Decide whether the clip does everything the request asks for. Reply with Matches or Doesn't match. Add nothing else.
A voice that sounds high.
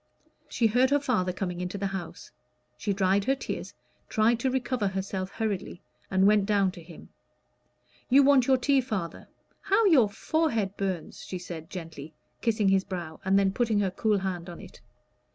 Matches